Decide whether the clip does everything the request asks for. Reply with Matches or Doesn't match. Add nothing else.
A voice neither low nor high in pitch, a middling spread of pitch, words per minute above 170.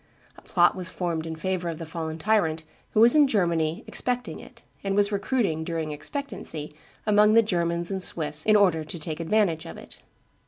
Matches